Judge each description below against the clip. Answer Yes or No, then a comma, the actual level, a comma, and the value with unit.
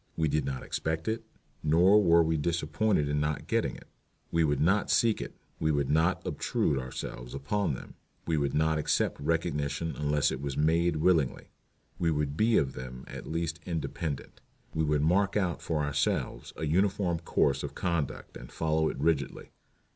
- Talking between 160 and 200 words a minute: Yes, average, 175 wpm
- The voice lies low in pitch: Yes, very low, 80 Hz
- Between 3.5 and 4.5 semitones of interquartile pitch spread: No, average, 2.7 semitones